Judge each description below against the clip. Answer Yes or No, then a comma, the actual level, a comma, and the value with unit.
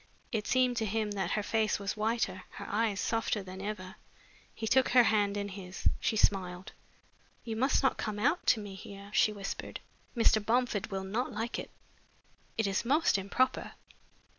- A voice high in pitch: Yes, high, 215 Hz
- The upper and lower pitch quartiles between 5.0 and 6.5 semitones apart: No, narrow, 2.6 semitones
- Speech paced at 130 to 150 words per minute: No, average, 175 wpm